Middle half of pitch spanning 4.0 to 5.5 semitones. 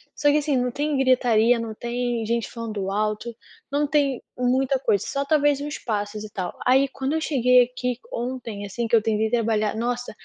No: average, 3.4 semitones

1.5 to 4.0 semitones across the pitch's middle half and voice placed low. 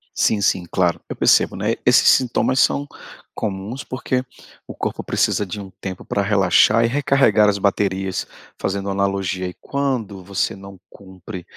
Yes: average, 3.2 semitones; low, 100 Hz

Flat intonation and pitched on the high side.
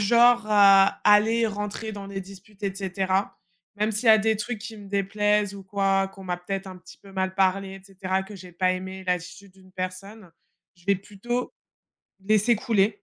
Yes: narrow, 1.8 semitones; high, 195 Hz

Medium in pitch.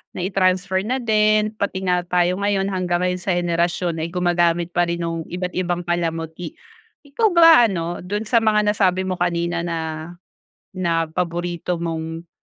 Yes: medium, 180 Hz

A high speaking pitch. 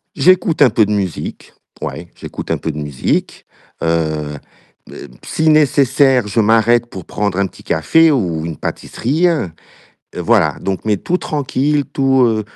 No: low, 110 Hz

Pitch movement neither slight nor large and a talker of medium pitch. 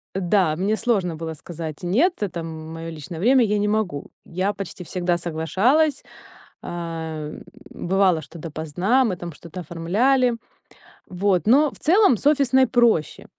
No: wide, 6.0 semitones; medium, 180 Hz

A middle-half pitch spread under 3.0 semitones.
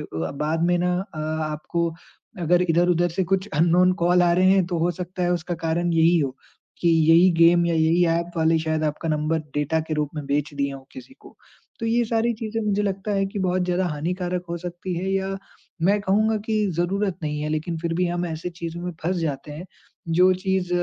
Yes: narrow, 2.5 semitones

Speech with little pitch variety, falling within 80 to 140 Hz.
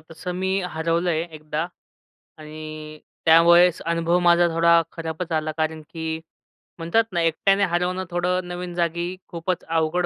No: narrow, 1.7 semitones; medium, 170 Hz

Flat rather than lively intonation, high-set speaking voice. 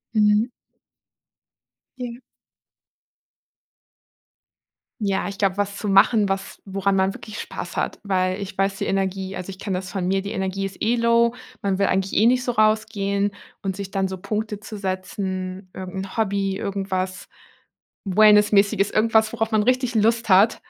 Yes: narrow, 2.0 semitones; high, 200 Hz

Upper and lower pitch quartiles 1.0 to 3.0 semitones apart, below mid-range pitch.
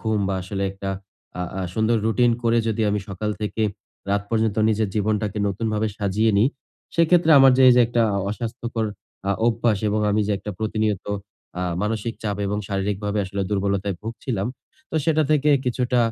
Yes: narrow, 2.4 semitones; low, 110 Hz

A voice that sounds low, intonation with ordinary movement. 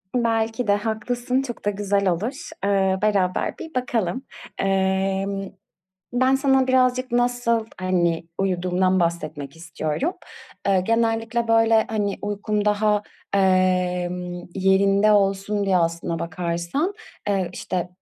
No: high, 200 Hz; average, 3.8 semitones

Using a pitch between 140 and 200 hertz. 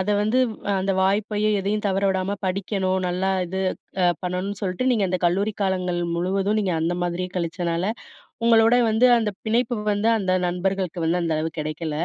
Yes: high, 190 Hz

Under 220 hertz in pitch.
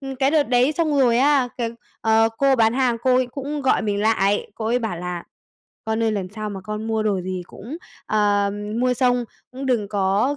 No: high, 230 Hz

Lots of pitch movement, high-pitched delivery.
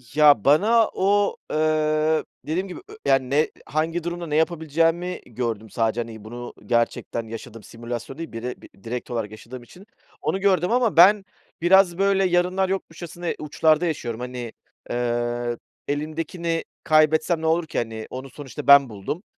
No: wide, 6.3 semitones; medium, 155 Hz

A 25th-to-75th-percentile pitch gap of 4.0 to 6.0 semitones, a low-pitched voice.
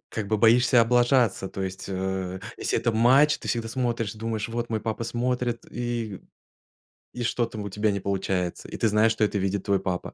No: average, 3.2 semitones; low, 110 Hz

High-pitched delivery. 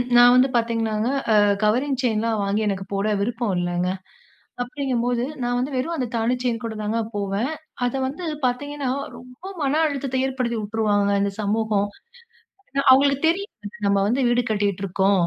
Yes: high, 235 Hz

